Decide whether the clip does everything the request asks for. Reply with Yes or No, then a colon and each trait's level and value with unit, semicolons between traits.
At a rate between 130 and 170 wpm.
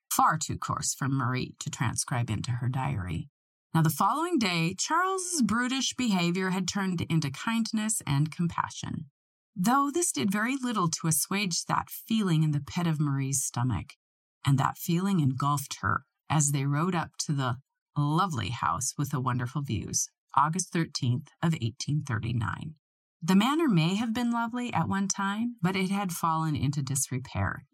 Yes: average, 165 wpm